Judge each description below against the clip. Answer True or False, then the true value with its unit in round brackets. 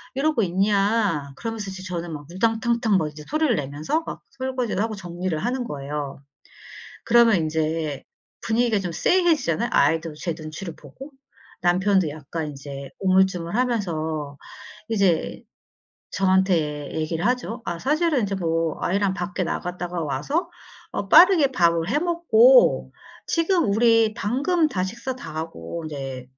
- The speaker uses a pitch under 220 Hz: True (190 Hz)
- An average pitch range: False (6.9 semitones)